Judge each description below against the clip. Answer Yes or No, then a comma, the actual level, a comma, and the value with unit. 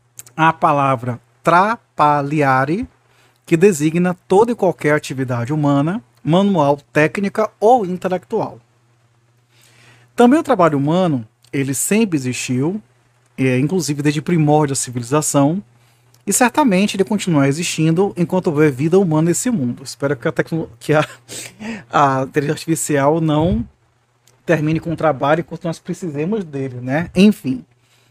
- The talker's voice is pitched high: No, medium, 150 Hz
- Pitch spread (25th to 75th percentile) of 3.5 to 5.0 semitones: No, wide, 5.4 semitones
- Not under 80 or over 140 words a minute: Yes, slow, 120 wpm